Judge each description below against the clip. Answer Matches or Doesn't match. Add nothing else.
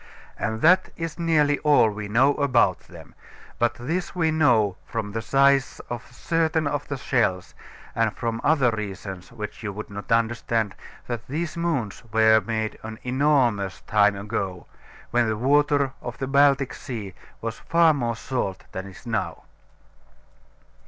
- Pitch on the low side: Matches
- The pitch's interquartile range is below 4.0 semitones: Doesn't match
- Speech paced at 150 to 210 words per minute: Matches